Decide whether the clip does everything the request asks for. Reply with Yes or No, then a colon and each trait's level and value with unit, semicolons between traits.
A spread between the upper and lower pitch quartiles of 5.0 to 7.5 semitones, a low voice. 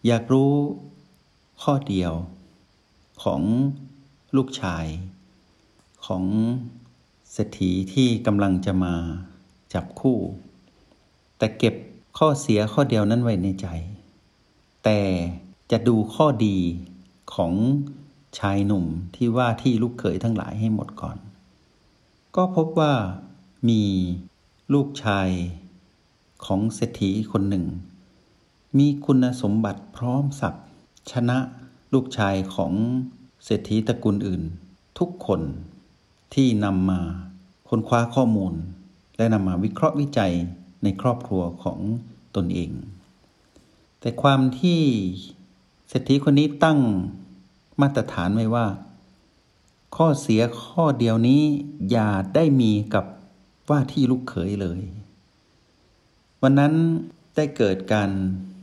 Yes: wide, 5.5 semitones; low, 105 Hz